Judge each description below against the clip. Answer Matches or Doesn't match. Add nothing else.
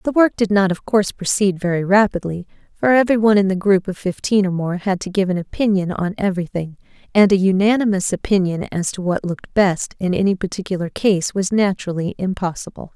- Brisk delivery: Doesn't match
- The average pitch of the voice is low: Doesn't match